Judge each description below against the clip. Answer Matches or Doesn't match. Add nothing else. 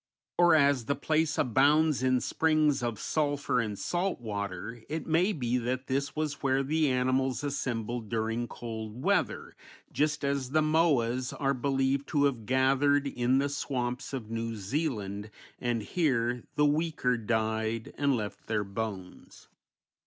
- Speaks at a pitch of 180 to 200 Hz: Doesn't match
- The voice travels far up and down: Doesn't match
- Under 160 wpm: Matches